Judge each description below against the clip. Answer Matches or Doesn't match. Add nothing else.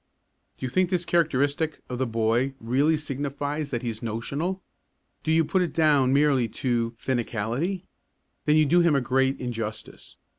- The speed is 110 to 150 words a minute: Doesn't match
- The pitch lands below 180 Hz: Matches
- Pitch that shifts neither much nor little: Matches